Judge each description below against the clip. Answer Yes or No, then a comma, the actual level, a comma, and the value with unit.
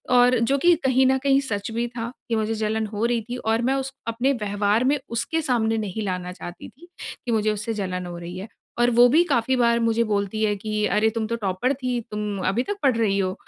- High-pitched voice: Yes, high, 225 Hz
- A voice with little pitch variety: No, average, 3.0 semitones